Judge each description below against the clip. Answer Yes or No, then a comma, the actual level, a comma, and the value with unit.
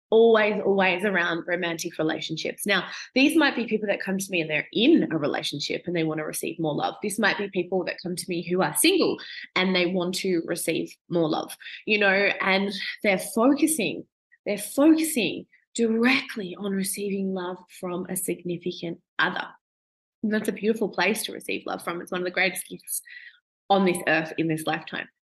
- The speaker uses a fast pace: No, average, 190 wpm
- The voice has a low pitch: No, high, 190 Hz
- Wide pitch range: No, average, 3.7 semitones